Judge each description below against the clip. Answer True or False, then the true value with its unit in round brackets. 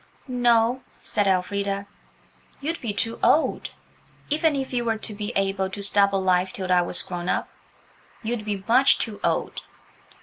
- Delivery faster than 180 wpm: False (155 wpm)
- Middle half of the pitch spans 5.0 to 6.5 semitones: False (3.5 semitones)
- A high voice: True (205 Hz)